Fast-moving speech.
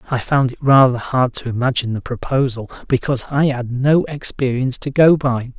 No: average, 185 wpm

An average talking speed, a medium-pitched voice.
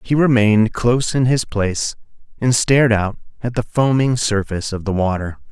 No: average, 175 wpm; low, 115 Hz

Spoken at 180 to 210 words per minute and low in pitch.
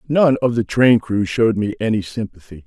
Yes: average, 200 wpm; low, 110 Hz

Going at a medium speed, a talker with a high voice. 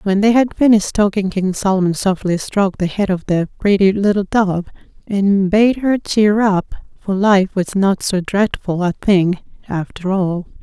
Yes: average, 175 wpm; high, 195 Hz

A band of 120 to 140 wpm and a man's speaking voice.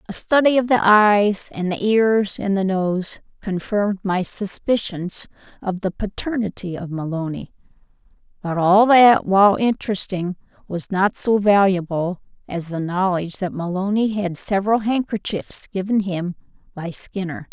No: slow, 135 wpm; female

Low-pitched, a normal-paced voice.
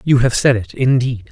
No: low, 125 Hz; fast, 230 wpm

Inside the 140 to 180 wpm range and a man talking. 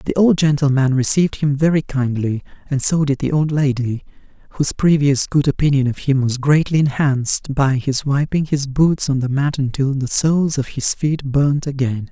No: average, 190 wpm; male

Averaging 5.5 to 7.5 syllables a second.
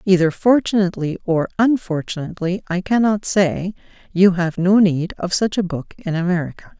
No: 5.1 syllables/s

